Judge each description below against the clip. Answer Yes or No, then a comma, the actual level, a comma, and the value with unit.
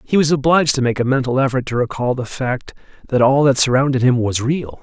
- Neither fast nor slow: No, fast, 235 wpm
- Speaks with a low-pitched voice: Yes, low, 130 Hz